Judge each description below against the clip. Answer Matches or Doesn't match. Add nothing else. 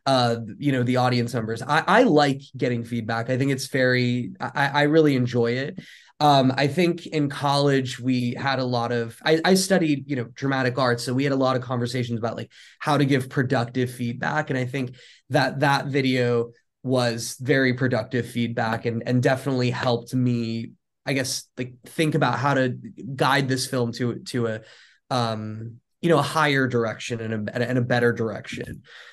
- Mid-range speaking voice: Doesn't match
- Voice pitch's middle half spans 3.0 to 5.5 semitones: Doesn't match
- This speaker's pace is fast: Doesn't match